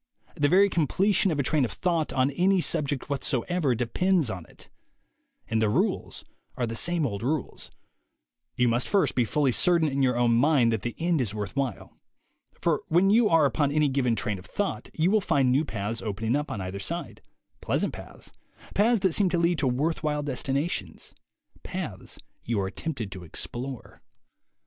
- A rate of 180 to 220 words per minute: Yes, average, 185 wpm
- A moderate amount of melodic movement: No, wide, 6.1 semitones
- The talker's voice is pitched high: No, medium, 140 Hz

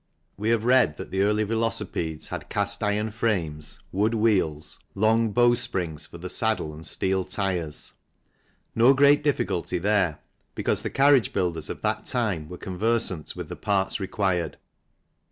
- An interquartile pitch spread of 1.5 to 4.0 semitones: No, average, 4.5 semitones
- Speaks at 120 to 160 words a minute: Yes, average, 155 wpm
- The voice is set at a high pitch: No, low, 100 Hz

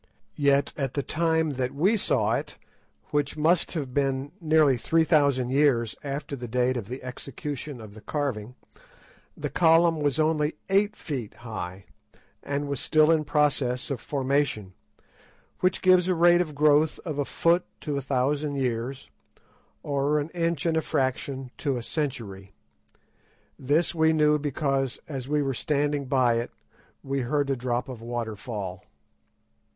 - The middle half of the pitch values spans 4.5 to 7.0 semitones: No, average, 3.4 semitones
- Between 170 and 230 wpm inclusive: No, average, 155 wpm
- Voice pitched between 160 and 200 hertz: No, medium, 140 Hz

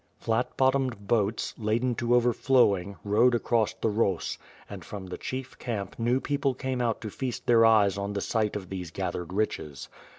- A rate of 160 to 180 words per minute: Yes, average, 175 wpm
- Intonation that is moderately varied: Yes, average, 3.5 semitones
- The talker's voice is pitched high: No, low, 115 Hz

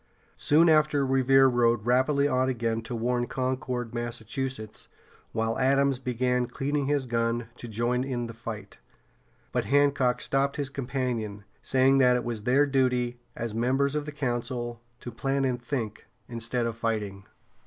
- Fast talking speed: No, average, 155 wpm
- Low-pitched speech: Yes, low, 125 Hz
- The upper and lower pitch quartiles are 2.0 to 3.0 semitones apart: Yes, narrow, 2.4 semitones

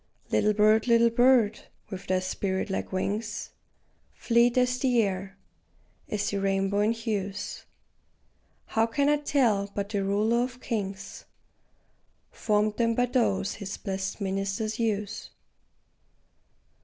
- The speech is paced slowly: Yes, slow, 125 wpm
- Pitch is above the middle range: Yes, high, 210 Hz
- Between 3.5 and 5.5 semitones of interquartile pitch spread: No, average, 2.9 semitones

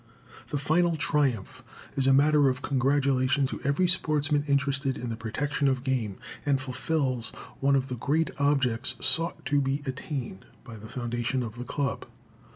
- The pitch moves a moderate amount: No, narrow, 2.2 semitones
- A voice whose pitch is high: No, low, 135 Hz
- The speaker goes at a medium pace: Yes, average, 160 wpm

